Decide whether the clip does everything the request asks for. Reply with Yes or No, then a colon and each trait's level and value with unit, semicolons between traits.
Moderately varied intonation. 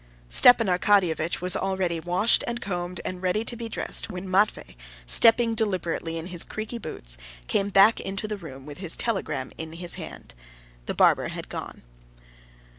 Yes: average, 4.2 semitones